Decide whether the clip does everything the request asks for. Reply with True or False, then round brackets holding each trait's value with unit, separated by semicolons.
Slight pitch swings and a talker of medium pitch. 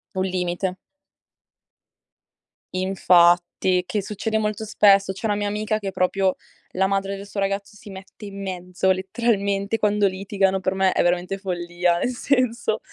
False (1.9 semitones; 195 Hz)